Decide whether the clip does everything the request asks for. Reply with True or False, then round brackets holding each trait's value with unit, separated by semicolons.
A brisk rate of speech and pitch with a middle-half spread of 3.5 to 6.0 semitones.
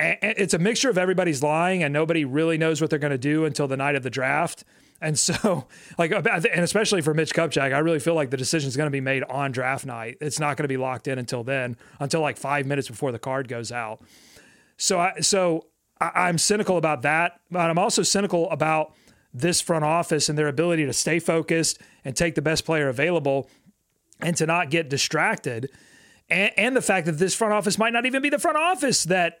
True (225 wpm; 4.1 semitones)